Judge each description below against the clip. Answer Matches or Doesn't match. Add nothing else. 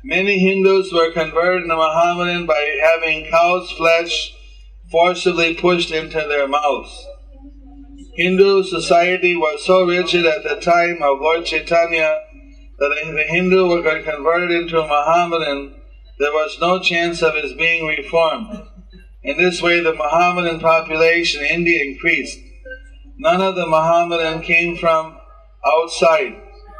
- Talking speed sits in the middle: Doesn't match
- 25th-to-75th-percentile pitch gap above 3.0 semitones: Doesn't match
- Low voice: Doesn't match